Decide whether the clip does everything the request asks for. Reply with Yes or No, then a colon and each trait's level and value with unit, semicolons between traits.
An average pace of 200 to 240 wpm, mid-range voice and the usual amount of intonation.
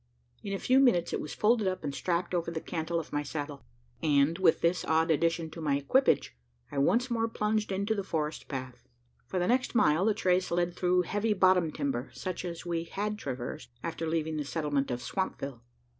Yes: fast, 205 wpm; medium, 170 Hz; average, 4.2 semitones